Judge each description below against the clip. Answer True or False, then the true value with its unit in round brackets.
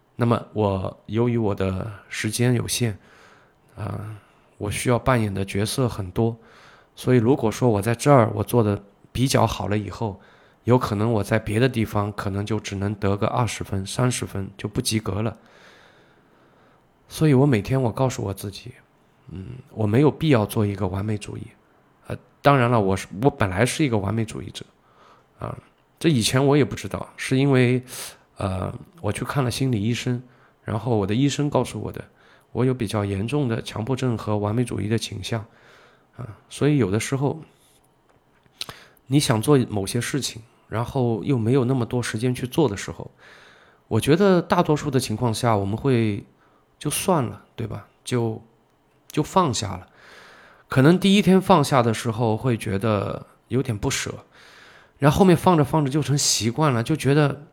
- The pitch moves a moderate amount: True (4.0 semitones)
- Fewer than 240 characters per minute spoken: False (255 characters per minute)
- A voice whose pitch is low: True (115 Hz)